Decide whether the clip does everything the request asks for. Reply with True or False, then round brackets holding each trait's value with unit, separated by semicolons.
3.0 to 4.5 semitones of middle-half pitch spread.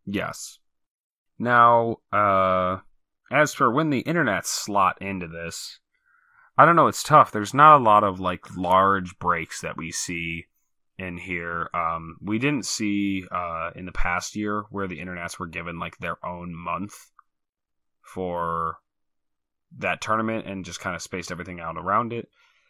True (3.5 semitones)